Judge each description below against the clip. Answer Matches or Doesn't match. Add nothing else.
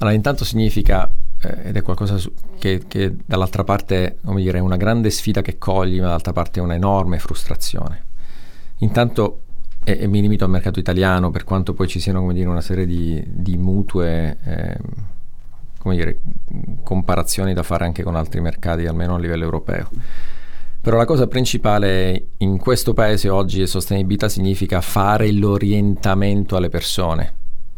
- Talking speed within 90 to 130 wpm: Doesn't match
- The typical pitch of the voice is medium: Doesn't match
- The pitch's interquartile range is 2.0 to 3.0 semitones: Matches